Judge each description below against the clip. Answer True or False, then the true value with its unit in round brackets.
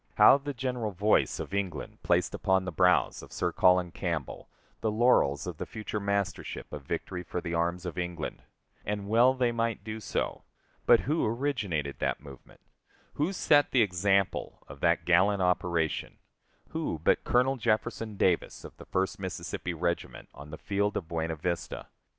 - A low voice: True (95 Hz)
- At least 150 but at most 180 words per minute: True (170 wpm)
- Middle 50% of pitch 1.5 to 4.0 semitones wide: False (4.8 semitones)